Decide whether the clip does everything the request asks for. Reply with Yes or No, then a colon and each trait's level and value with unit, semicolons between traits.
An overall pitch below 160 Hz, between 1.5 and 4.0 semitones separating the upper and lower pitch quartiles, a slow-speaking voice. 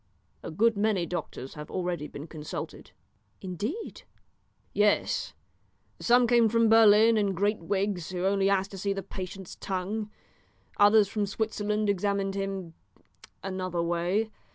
No: high, 195 Hz; narrow, 2.5 semitones; slow, 130 wpm